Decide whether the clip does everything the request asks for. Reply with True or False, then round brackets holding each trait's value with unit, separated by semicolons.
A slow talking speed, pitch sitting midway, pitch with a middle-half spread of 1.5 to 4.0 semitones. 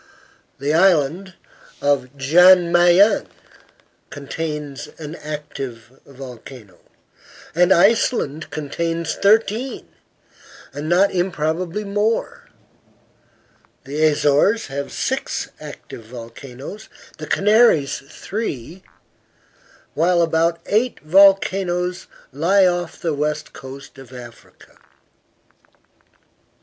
False (85 wpm; 160 Hz; 5.0 semitones)